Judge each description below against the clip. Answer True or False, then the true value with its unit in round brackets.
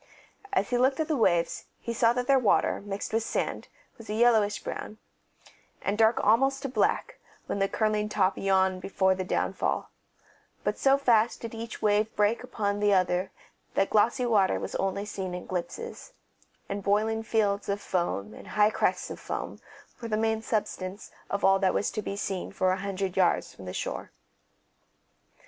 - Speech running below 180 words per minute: False (185 wpm)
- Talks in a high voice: True (210 Hz)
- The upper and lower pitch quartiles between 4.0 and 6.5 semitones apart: False (2.8 semitones)